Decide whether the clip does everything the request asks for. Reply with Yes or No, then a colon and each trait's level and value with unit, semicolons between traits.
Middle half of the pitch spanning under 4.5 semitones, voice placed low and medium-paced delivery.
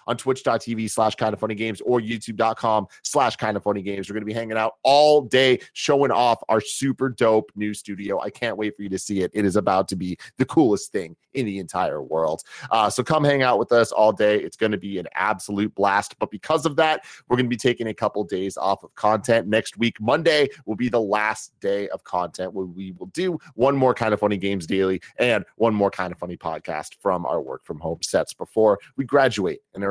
No: average, 3.6 semitones; low, 110 Hz; fast, 240 wpm